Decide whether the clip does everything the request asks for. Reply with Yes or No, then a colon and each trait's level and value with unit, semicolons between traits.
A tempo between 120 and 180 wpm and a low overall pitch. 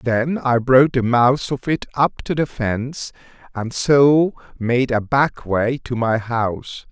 Yes: average, 175 wpm; low, 125 Hz